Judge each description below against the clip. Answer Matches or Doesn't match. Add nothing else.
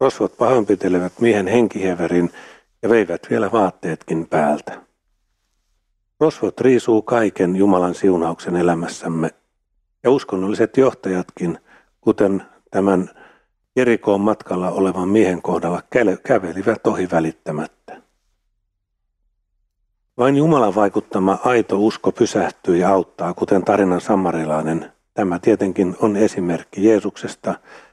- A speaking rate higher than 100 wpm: Doesn't match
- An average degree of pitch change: Matches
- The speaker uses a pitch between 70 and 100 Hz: Matches